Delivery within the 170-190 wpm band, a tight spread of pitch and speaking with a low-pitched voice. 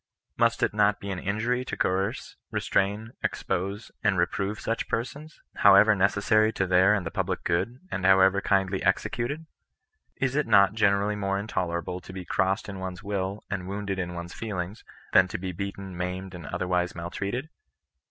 Yes: average, 175 wpm; narrow, 2.3 semitones; low, 100 Hz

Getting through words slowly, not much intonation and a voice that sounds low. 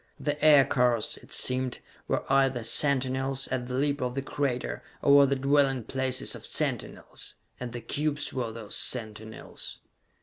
No: average, 155 wpm; narrow, 2.2 semitones; low, 130 Hz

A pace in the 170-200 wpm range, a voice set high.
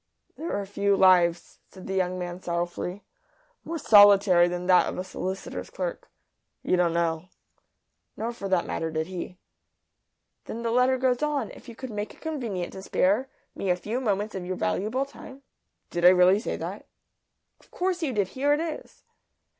Yes: average, 185 wpm; high, 195 Hz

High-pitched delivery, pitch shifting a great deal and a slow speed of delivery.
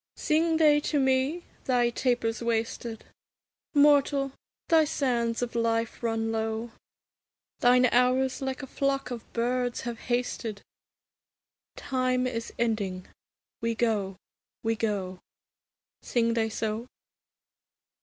No: high, 240 Hz; narrow, 2.6 semitones; slow, 110 wpm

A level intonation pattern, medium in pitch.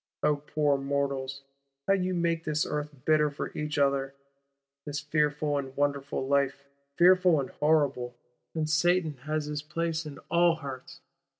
Yes: narrow, 2.2 semitones; medium, 150 Hz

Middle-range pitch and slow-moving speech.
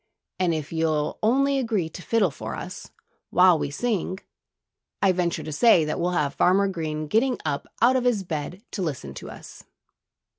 No: medium, 180 Hz; average, 180 wpm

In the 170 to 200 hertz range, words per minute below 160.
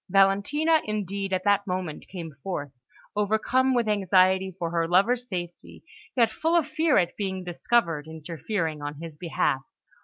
Yes: high, 190 Hz; average, 150 wpm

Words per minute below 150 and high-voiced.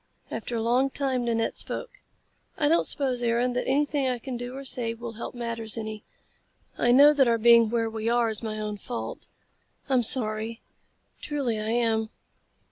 No: average, 180 wpm; high, 235 Hz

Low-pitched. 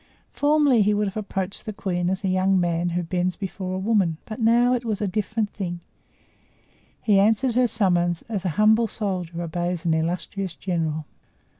No: high, 190 Hz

